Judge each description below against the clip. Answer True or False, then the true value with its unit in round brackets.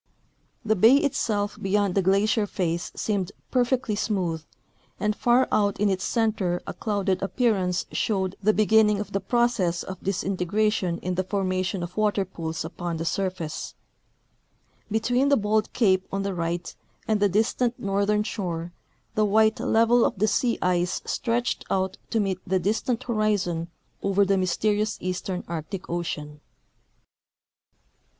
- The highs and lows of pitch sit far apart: False (2.9 semitones)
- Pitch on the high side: True (200 Hz)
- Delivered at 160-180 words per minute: False (145 wpm)